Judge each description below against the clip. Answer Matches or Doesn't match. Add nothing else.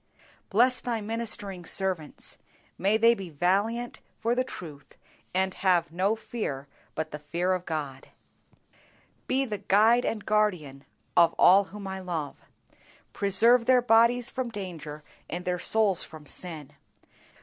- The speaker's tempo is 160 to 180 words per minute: Doesn't match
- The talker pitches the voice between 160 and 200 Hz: Matches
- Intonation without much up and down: Doesn't match